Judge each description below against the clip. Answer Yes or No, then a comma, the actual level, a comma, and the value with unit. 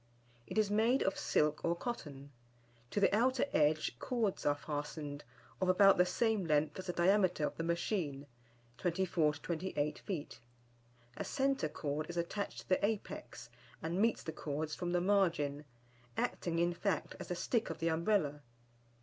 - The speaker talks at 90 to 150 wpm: No, average, 165 wpm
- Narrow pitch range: No, average, 4.8 semitones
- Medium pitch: Yes, medium, 170 Hz